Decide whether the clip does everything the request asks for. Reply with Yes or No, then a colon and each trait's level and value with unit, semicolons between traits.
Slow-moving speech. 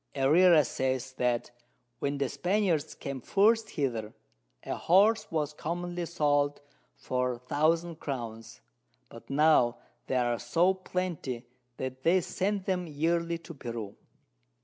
Yes: slow, 125 wpm